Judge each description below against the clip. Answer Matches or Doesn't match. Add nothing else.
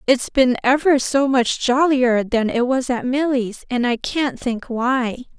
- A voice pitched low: Doesn't match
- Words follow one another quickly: Doesn't match